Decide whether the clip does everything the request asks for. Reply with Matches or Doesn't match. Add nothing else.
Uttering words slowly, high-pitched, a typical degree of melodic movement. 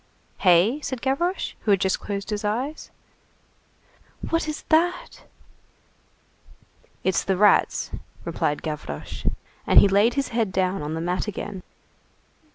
Doesn't match